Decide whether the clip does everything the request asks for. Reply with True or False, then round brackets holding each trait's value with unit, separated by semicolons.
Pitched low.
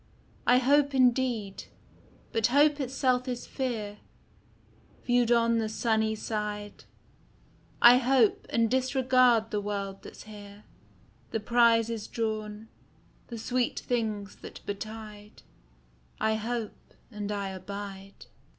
False (225 Hz)